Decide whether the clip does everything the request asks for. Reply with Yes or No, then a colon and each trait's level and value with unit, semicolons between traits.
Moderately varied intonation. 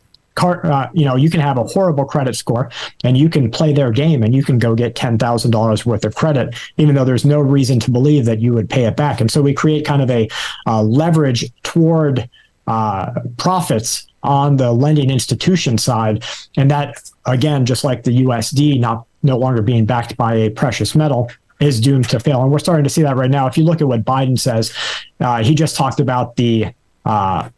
Yes: average, 3.7 semitones